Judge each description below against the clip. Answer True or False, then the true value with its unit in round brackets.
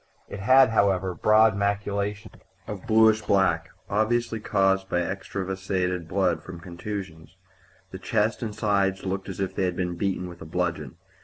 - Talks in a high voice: False (95 Hz)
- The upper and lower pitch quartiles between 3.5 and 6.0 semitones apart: False (2.4 semitones)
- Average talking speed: True (155 wpm)